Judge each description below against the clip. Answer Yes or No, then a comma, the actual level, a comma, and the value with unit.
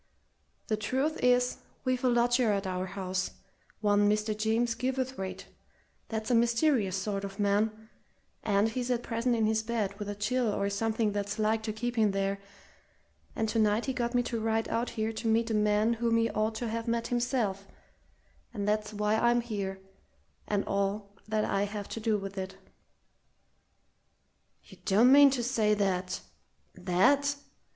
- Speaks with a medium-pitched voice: No, high, 220 Hz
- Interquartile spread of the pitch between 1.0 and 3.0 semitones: Yes, narrow, 2.6 semitones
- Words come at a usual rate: Yes, average, 170 wpm